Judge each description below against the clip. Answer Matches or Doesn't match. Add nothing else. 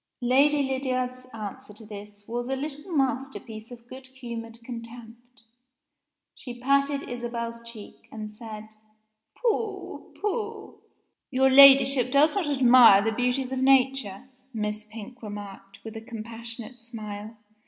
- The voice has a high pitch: Matches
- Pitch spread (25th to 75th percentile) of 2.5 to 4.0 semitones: Matches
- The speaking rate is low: Matches